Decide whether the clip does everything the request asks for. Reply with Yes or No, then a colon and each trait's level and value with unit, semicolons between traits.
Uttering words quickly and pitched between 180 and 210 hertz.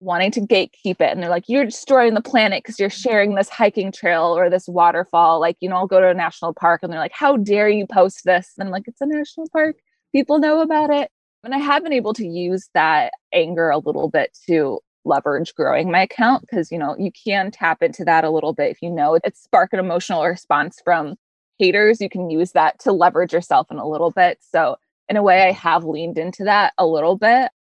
Yes: fast, 235 wpm; high, 190 Hz